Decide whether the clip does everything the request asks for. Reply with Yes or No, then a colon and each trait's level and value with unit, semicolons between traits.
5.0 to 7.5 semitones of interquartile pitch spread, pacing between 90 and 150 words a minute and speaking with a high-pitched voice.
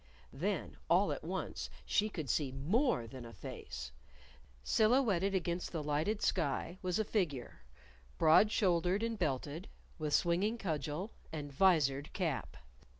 No: wide, 5.5 semitones; slow, 135 wpm; medium, 170 Hz